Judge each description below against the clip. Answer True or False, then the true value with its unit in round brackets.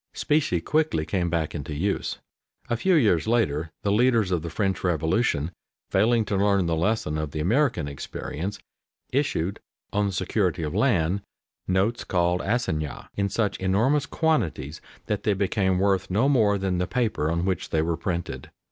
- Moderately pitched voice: False (95 Hz)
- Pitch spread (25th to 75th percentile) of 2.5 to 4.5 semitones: False (4.9 semitones)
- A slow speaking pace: False (165 wpm)